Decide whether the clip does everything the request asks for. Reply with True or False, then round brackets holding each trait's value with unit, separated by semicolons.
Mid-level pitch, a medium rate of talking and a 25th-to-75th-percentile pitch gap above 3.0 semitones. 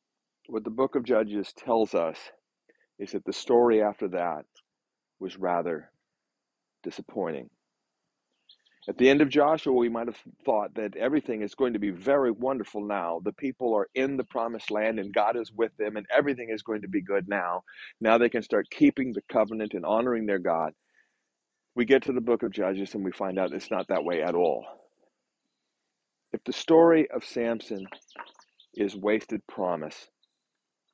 False (115 Hz; 175 wpm; 3.8 semitones)